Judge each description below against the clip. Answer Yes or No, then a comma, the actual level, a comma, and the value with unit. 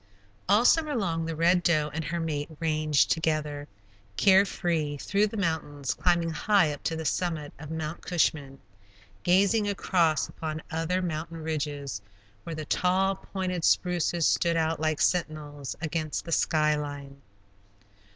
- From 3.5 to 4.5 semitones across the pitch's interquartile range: No, average, 2.7 semitones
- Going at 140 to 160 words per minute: Yes, average, 145 wpm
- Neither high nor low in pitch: Yes, medium, 160 Hz